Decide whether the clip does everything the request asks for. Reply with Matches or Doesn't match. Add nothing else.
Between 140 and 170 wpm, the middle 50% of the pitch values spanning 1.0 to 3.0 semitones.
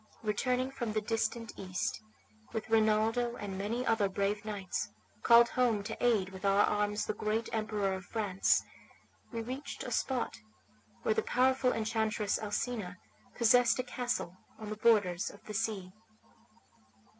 Matches